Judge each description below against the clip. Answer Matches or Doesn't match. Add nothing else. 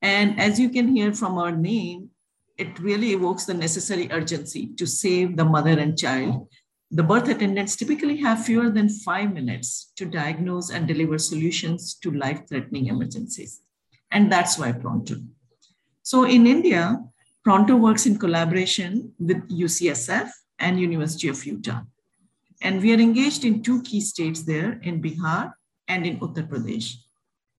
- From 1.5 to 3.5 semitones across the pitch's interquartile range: Doesn't match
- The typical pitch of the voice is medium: Matches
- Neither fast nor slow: Matches